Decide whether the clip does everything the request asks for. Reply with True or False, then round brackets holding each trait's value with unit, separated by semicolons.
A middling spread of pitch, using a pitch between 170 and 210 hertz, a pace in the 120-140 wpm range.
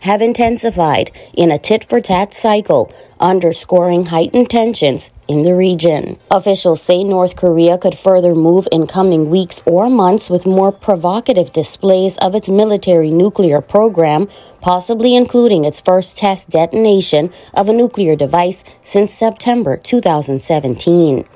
True (3.8 semitones; 185 Hz; 135 wpm)